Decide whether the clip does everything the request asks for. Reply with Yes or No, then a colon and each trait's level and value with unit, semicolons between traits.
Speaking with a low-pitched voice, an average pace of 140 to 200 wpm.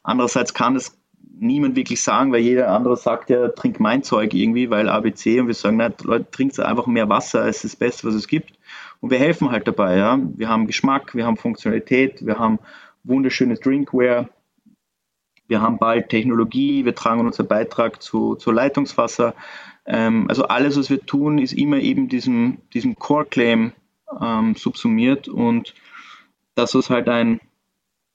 Yes: low, 130 Hz; average, 170 wpm